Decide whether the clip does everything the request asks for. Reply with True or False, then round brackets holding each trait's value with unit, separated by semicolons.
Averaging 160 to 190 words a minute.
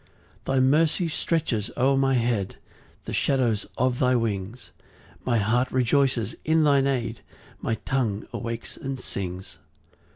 False (135 wpm)